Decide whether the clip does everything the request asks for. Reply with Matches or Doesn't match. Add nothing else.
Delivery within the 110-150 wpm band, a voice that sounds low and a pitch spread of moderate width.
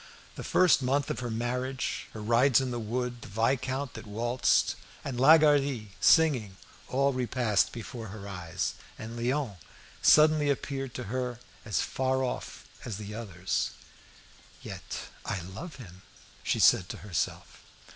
Matches